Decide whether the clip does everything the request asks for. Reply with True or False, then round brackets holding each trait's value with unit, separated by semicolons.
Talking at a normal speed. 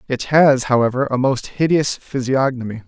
True (145 wpm)